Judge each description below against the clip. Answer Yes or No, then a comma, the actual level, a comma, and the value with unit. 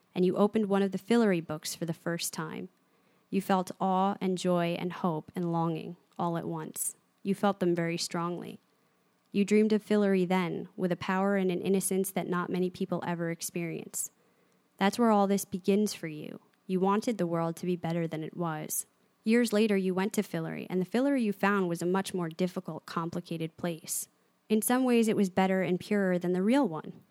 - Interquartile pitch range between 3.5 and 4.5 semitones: No, average, 2.8 semitones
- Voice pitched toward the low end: No, medium, 185 Hz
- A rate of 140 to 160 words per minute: No, fast, 205 wpm